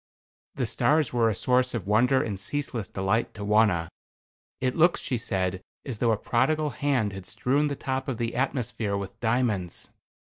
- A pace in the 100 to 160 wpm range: No, average, 175 wpm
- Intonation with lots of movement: No, average, 4.4 semitones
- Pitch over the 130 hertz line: No, low, 115 Hz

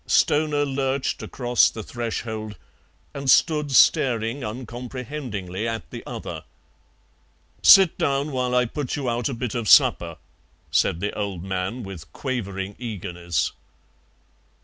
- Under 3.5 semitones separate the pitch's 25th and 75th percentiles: No, average, 4.5 semitones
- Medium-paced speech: No, slow, 125 wpm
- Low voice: Yes, low, 120 Hz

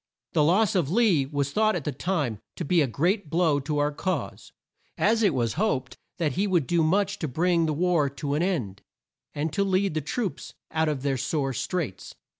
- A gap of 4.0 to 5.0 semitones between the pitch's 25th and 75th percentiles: Yes, average, 4.6 semitones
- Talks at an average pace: No, fast, 210 wpm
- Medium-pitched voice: Yes, medium, 160 Hz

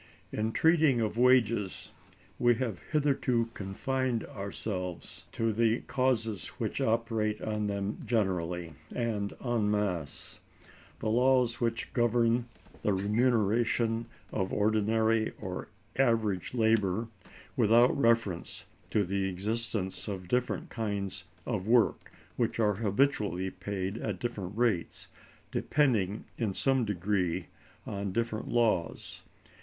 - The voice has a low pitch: Yes, low, 110 Hz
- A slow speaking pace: Yes, slow, 110 wpm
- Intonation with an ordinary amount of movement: Yes, average, 3.1 semitones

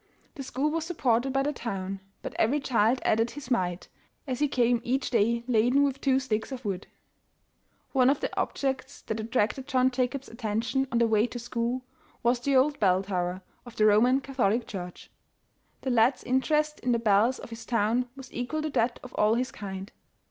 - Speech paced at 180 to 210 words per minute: Yes, average, 195 wpm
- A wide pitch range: No, average, 3.3 semitones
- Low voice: No, high, 245 Hz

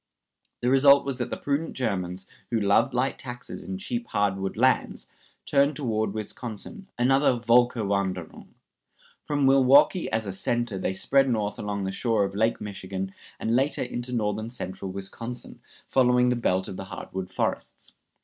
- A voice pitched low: Yes, low, 115 Hz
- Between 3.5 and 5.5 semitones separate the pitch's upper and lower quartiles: Yes, average, 4.8 semitones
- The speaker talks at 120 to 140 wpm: No, average, 160 wpm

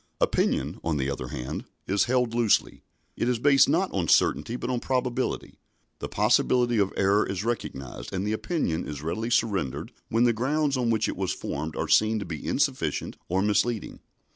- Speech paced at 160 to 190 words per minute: Yes, average, 185 wpm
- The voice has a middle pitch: No, low, 110 Hz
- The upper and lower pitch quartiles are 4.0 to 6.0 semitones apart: Yes, average, 4.9 semitones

